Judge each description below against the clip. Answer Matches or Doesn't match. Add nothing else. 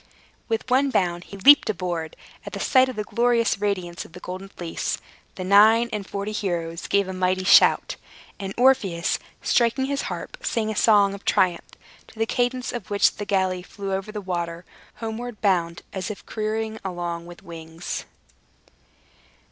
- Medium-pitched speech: Doesn't match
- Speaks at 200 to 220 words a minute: Doesn't match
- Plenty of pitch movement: Doesn't match